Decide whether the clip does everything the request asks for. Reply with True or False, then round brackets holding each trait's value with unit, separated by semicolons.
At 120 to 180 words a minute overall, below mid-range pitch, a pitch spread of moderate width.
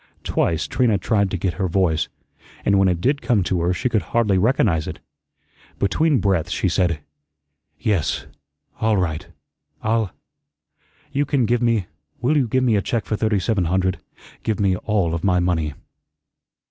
True (170 wpm; 100 Hz; 4.2 semitones)